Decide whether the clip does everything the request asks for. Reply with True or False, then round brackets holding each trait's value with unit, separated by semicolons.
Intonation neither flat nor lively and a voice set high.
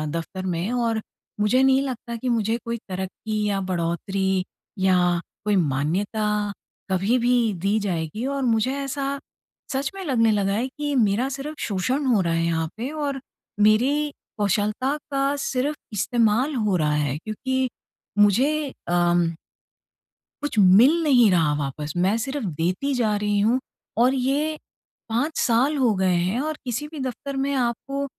False (5.8 semitones; 225 Hz)